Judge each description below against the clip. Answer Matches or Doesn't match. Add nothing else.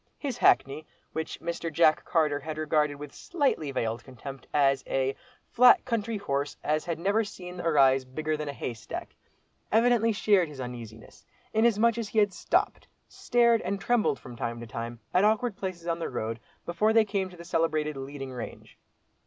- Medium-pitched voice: Matches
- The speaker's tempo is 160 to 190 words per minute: Matches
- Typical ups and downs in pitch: Doesn't match